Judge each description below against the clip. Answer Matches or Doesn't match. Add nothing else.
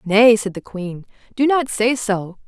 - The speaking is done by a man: Doesn't match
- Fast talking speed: Doesn't match